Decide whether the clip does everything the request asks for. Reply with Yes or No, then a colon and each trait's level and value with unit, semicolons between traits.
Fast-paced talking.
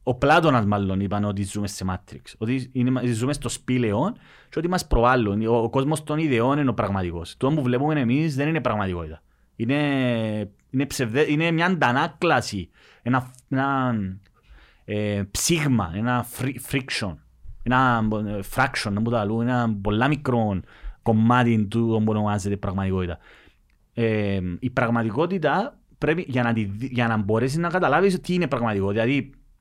No: average, 145 wpm